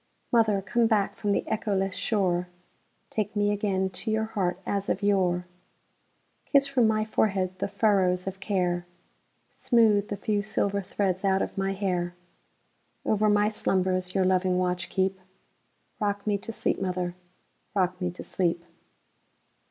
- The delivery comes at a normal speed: No, slow, 130 wpm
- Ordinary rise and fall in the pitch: No, narrow, 2.3 semitones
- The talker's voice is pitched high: Yes, high, 195 Hz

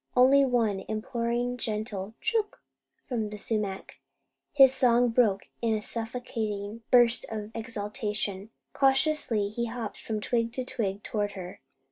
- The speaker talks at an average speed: No, slow, 130 wpm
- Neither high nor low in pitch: No, high, 225 Hz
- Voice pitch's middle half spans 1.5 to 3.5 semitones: Yes, average, 2.9 semitones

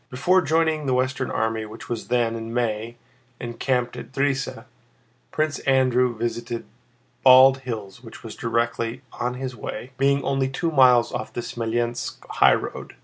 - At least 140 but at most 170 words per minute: Yes, average, 145 wpm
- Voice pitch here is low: Yes, low, 125 Hz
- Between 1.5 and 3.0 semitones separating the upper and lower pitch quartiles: Yes, narrow, 2.4 semitones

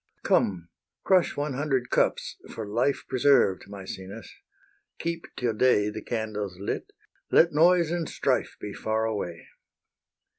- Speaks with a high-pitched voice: No, low, 115 Hz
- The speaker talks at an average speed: No, slow, 125 wpm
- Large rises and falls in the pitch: Yes, wide, 5.9 semitones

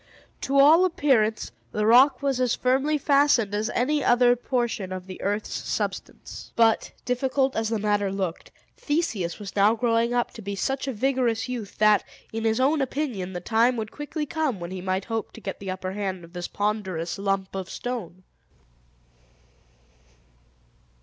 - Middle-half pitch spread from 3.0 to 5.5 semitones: Yes, average, 4.9 semitones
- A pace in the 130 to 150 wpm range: No, average, 170 wpm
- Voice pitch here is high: Yes, high, 225 Hz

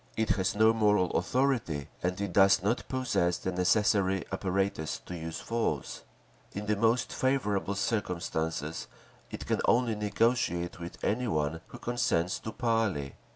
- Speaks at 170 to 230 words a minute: No, average, 145 wpm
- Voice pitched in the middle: No, low, 100 Hz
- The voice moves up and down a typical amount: Yes, average, 4.4 semitones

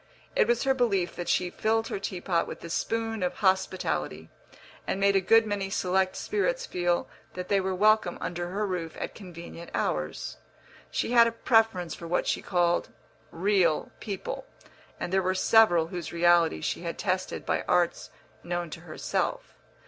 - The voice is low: No, medium, 185 Hz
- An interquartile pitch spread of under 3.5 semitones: No, average, 3.8 semitones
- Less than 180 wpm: Yes, average, 170 wpm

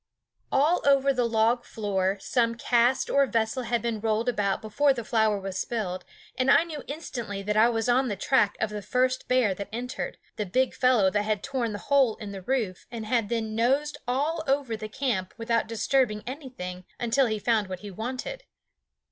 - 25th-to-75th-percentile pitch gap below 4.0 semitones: Yes, average, 3.6 semitones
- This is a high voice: Yes, high, 230 Hz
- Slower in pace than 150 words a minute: No, average, 195 wpm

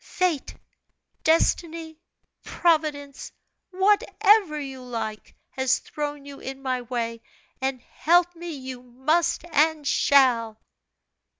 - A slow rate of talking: Yes, slow, 100 wpm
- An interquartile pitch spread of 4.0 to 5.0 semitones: Yes, average, 4.3 semitones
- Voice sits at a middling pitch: No, very high, 285 Hz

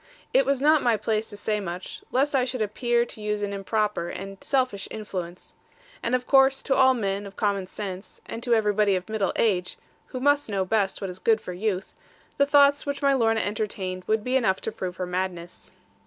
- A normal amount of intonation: Yes, average, 4.7 semitones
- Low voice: No, high, 215 Hz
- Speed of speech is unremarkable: No, fast, 210 wpm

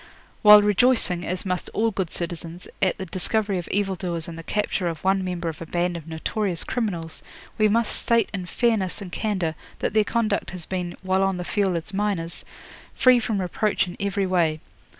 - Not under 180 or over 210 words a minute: Yes, average, 195 wpm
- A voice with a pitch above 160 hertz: Yes, high, 190 Hz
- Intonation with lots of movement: No, average, 3.2 semitones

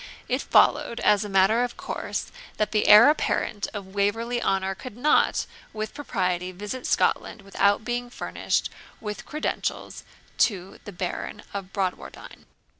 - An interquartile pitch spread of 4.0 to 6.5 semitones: No, average, 3.5 semitones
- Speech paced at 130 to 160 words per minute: Yes, average, 140 wpm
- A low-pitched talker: No, high, 205 Hz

